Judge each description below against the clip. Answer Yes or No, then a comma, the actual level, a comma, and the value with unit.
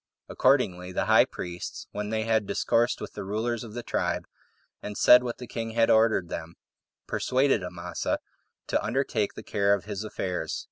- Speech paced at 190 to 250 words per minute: No, average, 175 wpm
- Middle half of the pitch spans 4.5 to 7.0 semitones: No, average, 3.6 semitones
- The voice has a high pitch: No, low, 110 Hz